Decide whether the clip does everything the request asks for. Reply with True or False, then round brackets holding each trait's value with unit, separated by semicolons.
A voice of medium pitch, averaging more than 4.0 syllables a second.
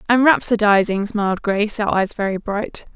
False (210 Hz; 5.2 syllables/s)